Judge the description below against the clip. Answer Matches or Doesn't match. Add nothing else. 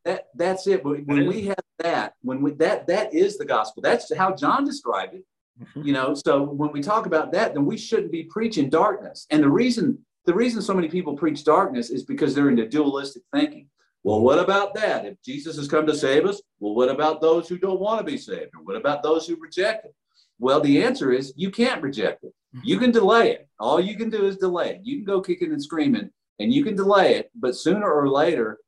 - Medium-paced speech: Doesn't match